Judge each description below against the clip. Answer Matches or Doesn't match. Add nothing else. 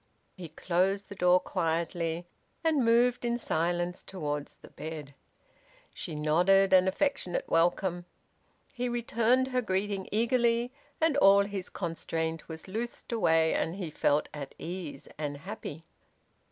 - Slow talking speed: Matches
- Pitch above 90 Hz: Matches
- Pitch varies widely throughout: Matches